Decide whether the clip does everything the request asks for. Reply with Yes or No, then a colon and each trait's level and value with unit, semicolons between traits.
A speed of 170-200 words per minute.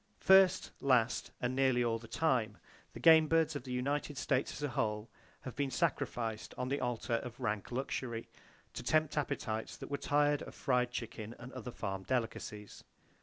Yes: average, 175 wpm